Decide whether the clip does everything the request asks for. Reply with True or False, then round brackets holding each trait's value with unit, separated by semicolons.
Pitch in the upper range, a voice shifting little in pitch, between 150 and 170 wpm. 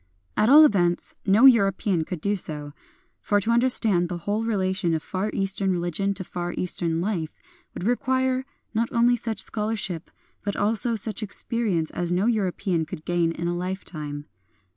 False (195 Hz; 4.2 semitones; 165 wpm)